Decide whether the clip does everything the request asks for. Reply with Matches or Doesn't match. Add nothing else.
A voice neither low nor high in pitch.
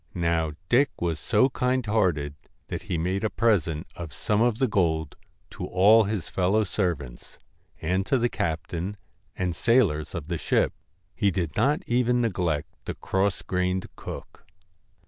Doesn't match